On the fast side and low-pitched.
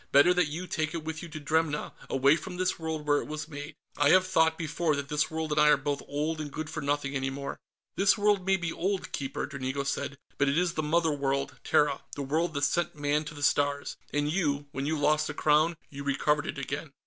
No: fast, 245 wpm; medium, 150 Hz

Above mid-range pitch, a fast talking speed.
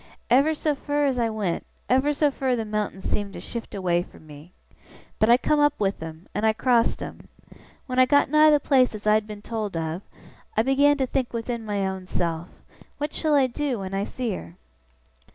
Yes: high, 230 Hz; fast, 215 wpm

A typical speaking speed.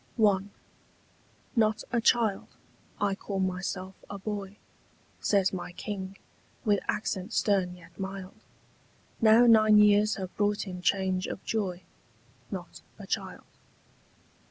No: slow, 120 wpm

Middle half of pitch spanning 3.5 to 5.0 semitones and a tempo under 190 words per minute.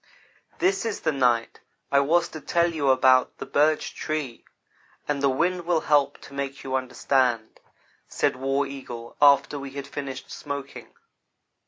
No: average, 2.7 semitones; average, 155 wpm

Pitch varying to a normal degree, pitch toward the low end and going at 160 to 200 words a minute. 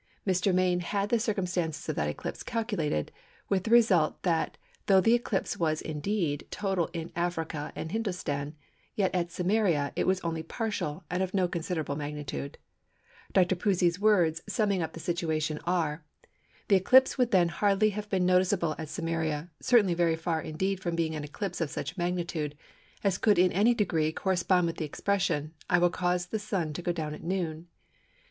No: average, 3.3 semitones; medium, 175 Hz; average, 175 wpm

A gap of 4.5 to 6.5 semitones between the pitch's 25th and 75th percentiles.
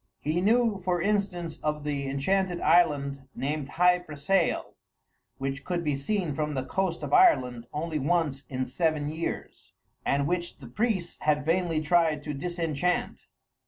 No: average, 3.9 semitones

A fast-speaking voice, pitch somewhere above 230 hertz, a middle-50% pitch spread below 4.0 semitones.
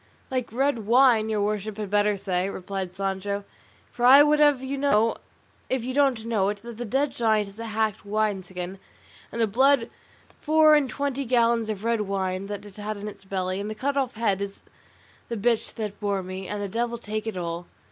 No: fast, 210 wpm; high, 215 Hz; average, 3.4 semitones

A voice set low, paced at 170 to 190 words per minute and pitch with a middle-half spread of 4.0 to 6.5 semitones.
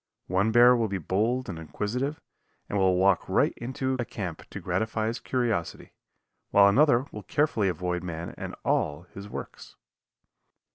No: low, 105 Hz; average, 155 wpm; average, 4.7 semitones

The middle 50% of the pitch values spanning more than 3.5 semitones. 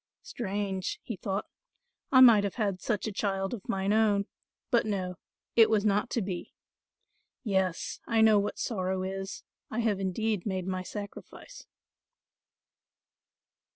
No: narrow, 2.4 semitones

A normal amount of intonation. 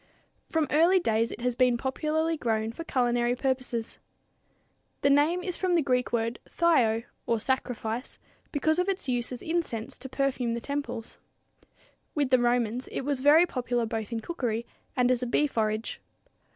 Yes: average, 4.2 semitones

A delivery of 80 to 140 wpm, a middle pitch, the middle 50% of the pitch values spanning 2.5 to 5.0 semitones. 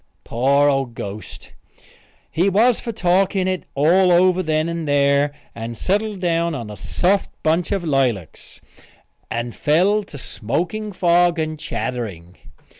No: slow, 135 wpm; medium, 160 Hz; wide, 5.4 semitones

